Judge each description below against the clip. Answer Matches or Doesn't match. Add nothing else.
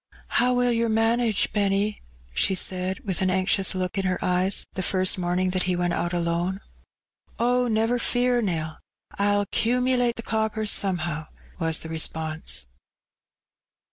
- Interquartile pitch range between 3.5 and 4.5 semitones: Matches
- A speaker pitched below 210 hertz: Matches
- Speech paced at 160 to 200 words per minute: Doesn't match